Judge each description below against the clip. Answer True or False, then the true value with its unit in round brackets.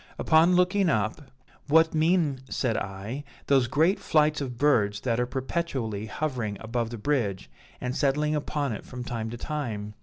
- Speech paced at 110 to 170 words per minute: True (160 wpm)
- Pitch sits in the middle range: False (130 Hz)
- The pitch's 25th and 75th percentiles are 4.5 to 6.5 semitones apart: True (5.3 semitones)